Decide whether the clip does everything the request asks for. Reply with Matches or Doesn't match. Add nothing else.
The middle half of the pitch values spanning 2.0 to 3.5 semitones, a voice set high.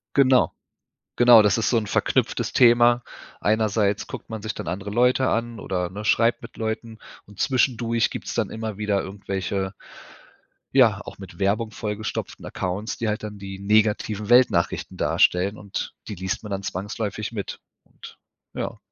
Doesn't match